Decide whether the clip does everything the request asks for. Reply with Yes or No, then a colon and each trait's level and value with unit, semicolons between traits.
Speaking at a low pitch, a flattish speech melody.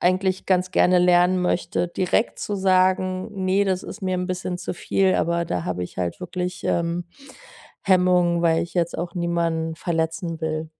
No: medium, 180 Hz; narrow, 1.6 semitones